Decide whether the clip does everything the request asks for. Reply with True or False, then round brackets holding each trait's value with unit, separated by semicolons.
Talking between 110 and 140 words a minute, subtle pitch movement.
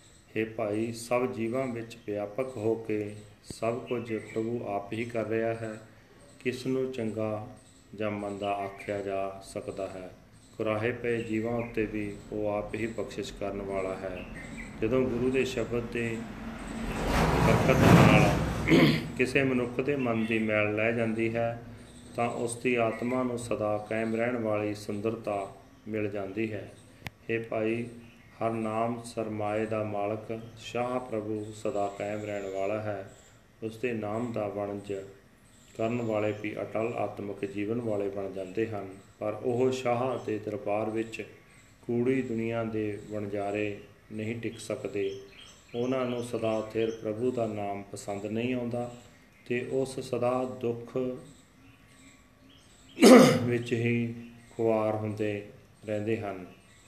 True (135 wpm; 2.3 semitones)